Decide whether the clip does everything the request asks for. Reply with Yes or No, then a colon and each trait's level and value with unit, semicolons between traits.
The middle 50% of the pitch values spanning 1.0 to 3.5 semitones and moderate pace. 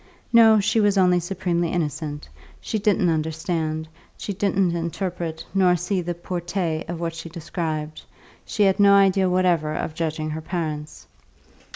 Yes: average, 3.1 semitones; average, 150 wpm